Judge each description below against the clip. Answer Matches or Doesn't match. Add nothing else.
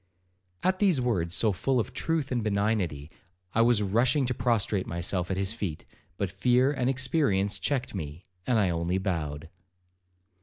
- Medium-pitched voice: Doesn't match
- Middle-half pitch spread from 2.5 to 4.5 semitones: Doesn't match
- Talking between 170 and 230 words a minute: Doesn't match